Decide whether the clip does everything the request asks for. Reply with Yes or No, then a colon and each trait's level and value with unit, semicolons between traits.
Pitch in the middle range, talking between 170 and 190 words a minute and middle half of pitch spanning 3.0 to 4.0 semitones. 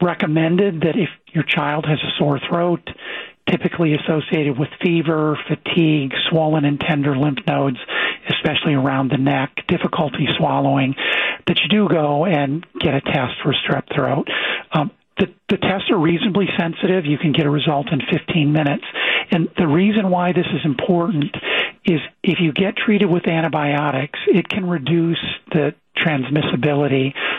No: medium, 160 Hz; average, 155 wpm; average, 3.4 semitones